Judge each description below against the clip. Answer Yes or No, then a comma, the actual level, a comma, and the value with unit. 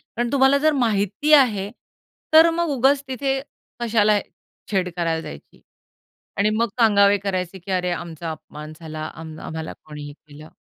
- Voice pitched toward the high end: Yes, high, 200 Hz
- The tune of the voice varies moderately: No, wide, 7.5 semitones